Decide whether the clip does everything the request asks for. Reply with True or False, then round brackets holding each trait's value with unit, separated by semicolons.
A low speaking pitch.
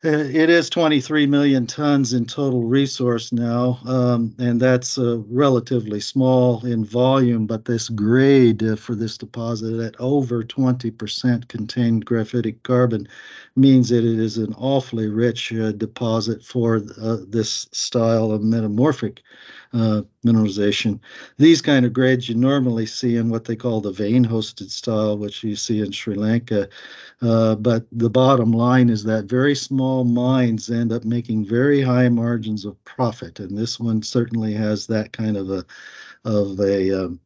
True (115 Hz)